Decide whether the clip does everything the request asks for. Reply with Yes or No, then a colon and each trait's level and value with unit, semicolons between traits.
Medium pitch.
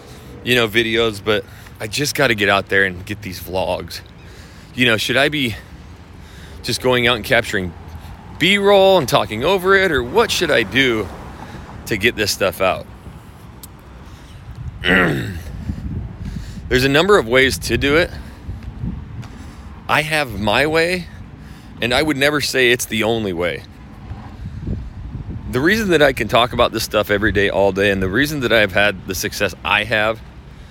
No: low, 105 Hz